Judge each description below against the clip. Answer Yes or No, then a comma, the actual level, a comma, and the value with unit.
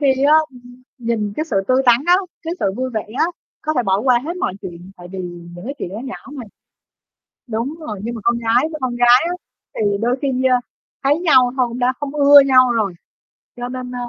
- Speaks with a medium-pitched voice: No, very high, 250 Hz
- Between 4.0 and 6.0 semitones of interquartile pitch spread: No, average, 3.2 semitones